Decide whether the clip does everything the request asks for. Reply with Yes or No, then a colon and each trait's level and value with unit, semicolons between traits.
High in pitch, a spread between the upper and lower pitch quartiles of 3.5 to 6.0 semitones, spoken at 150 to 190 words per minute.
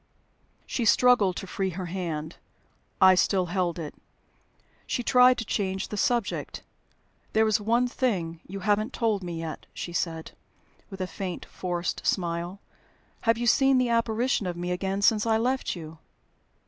Yes: high, 195 Hz; average, 4.5 semitones; average, 160 wpm